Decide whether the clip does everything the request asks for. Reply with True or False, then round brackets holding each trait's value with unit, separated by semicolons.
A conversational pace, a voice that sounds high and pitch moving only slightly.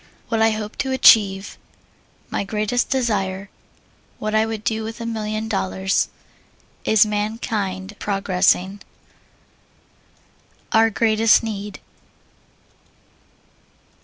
False (95 wpm; 215 Hz; 2.0 semitones)